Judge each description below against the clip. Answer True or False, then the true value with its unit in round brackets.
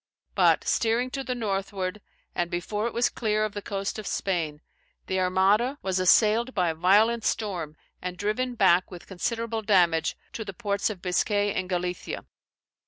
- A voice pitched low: False (200 Hz)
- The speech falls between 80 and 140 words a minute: False (170 wpm)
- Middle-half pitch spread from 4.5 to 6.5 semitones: False (3.3 semitones)